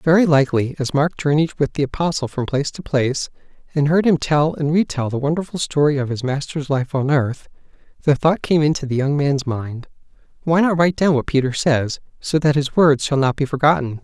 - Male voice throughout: Yes, male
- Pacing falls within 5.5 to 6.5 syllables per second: Yes, 5.6 syllables/s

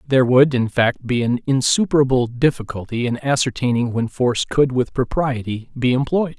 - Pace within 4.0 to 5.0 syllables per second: No, 5.2 syllables/s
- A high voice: No, low, 130 Hz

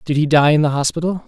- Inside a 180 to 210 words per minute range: No, fast, 280 wpm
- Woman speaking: No, male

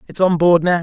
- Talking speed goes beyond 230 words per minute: Yes, fast, 360 wpm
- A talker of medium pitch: Yes, medium, 175 Hz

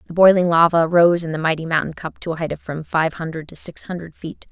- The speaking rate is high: Yes, fast, 265 wpm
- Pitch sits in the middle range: Yes, medium, 165 Hz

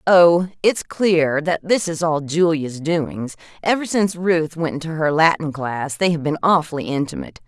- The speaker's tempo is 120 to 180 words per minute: Yes, average, 175 wpm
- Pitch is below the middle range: No, medium, 160 Hz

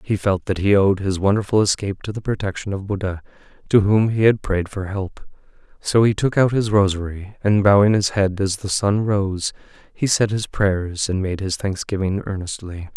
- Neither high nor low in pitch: No, low, 100 Hz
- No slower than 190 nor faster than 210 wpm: Yes, average, 200 wpm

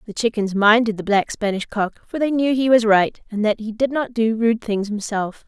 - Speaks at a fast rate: Yes, fast, 240 wpm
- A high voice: Yes, high, 220 Hz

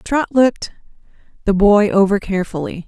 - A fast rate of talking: No, slow, 125 wpm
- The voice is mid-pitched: No, high, 205 Hz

